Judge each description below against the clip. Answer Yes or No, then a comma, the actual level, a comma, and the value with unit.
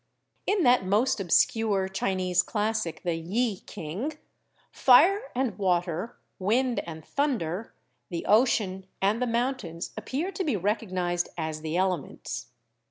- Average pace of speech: No, slow, 125 wpm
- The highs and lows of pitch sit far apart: Yes, wide, 5.7 semitones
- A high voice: Yes, high, 200 Hz